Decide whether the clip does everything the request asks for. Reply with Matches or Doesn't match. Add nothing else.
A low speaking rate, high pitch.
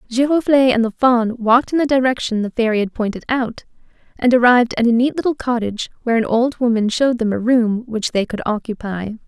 Doesn't match